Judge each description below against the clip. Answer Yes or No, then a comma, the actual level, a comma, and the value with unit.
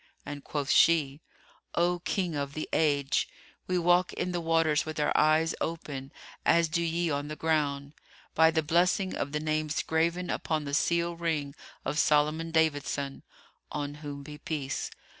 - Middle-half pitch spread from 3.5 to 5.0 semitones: No, narrow, 2.4 semitones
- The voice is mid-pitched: Yes, medium, 155 Hz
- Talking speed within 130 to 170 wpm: Yes, average, 165 wpm